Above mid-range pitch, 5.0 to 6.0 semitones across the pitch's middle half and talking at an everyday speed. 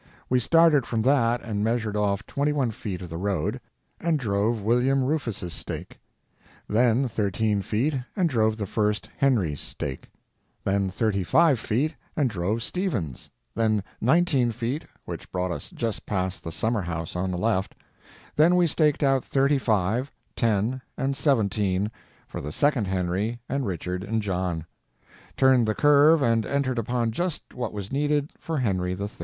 No: low, 115 Hz; wide, 5.5 semitones; average, 160 wpm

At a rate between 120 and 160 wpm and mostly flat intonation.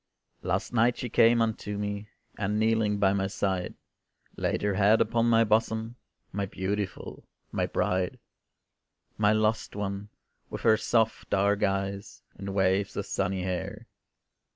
Yes: average, 140 wpm; narrow, 2.1 semitones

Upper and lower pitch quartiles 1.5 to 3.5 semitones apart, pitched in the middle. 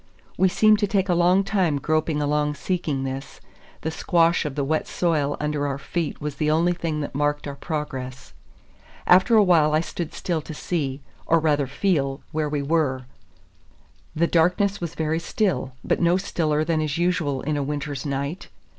Yes: average, 3.1 semitones; medium, 155 Hz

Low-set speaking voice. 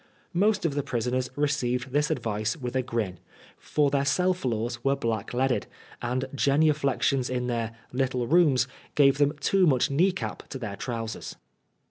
Yes: low, 130 Hz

